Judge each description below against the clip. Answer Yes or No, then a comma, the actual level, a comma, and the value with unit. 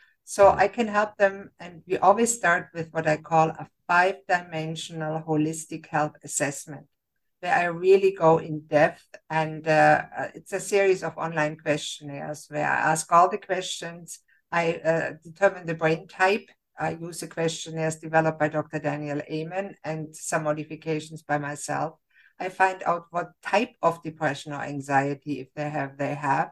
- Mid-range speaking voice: Yes, medium, 160 Hz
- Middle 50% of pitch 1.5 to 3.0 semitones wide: Yes, narrow, 2.5 semitones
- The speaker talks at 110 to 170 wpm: Yes, average, 165 wpm